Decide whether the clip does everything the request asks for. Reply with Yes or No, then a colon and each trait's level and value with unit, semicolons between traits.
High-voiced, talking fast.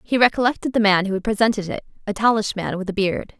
Yes: high, 210 Hz; fast, 250 wpm